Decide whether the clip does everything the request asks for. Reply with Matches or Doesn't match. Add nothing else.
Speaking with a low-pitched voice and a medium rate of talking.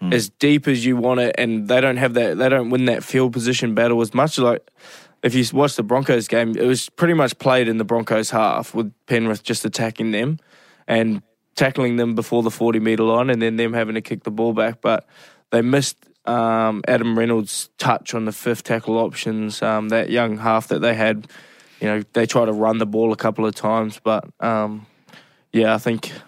Doesn't match